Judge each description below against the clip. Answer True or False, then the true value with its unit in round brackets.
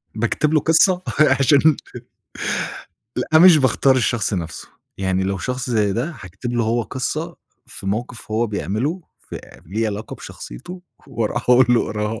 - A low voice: True (120 Hz)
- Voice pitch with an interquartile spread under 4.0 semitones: False (4.8 semitones)